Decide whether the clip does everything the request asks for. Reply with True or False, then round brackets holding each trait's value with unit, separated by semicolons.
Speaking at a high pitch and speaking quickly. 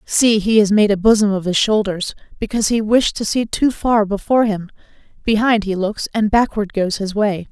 True (210 Hz; 210 wpm)